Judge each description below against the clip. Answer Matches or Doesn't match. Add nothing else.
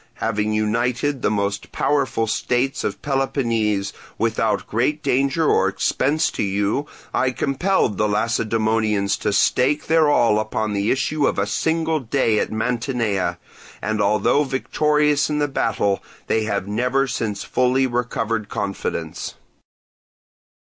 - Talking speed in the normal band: Doesn't match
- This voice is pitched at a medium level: Doesn't match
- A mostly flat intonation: Doesn't match